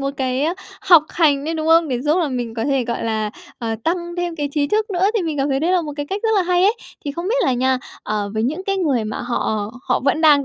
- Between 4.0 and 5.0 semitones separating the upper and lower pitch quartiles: No, wide, 5.5 semitones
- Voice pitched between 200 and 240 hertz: No, very high, 295 Hz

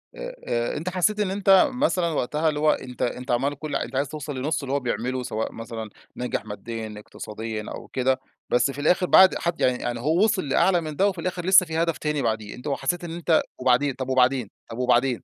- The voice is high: No, medium, 140 Hz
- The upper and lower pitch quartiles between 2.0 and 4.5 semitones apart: No, wide, 5.5 semitones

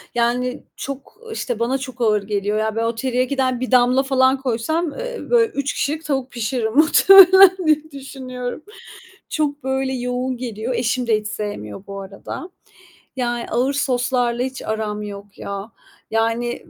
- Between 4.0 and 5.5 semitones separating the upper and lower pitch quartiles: No, average, 3.2 semitones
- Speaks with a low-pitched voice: No, very high, 250 Hz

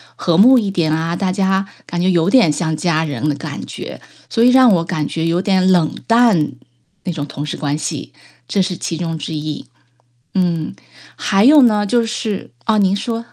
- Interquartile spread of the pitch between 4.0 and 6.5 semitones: Yes, average, 4.5 semitones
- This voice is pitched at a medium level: Yes, medium, 180 Hz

